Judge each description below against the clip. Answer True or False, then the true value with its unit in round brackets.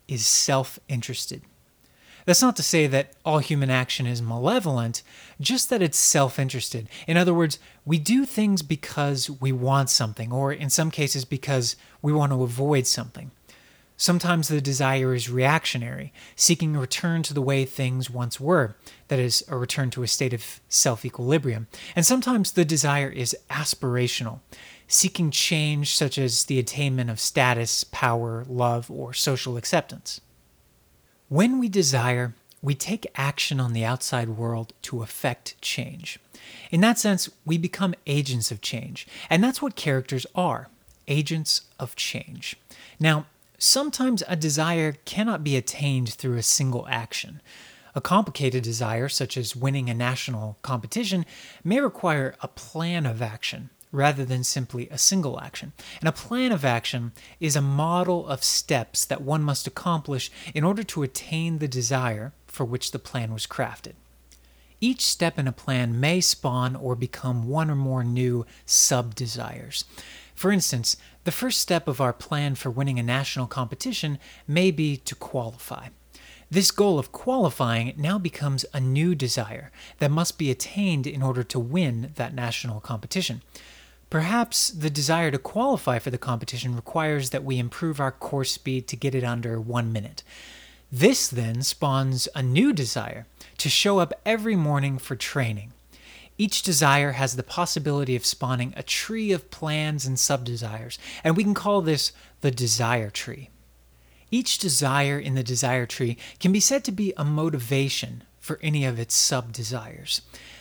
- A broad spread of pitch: False (4.5 semitones)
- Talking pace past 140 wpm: True (160 wpm)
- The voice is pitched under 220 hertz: True (135 Hz)